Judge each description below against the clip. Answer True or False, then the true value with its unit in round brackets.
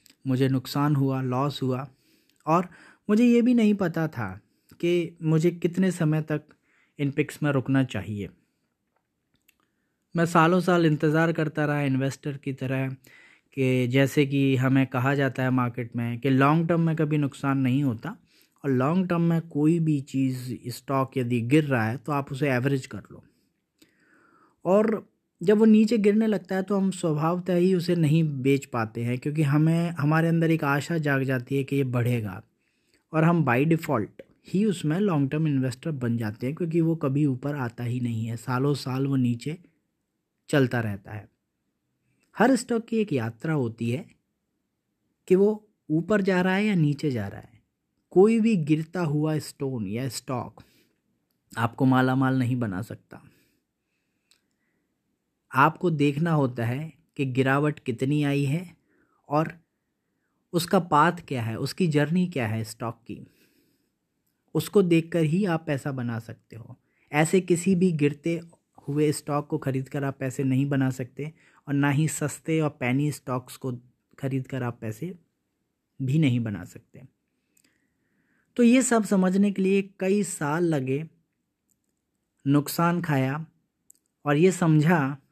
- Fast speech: False (155 wpm)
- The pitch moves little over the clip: False (4.3 semitones)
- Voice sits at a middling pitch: True (145 Hz)